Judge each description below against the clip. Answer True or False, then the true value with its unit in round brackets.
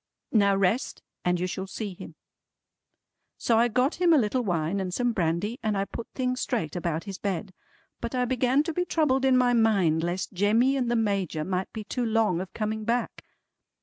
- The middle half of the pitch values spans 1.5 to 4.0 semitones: False (4.8 semitones)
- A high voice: True (215 Hz)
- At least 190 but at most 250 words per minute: True (200 wpm)